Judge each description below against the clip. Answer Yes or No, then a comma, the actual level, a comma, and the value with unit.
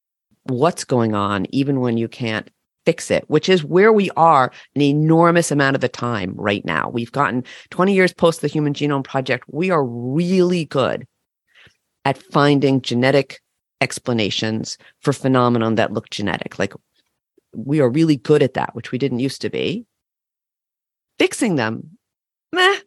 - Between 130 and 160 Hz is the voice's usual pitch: Yes, medium, 140 Hz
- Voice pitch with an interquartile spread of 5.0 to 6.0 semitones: Yes, average, 5.3 semitones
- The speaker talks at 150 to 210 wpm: Yes, average, 155 wpm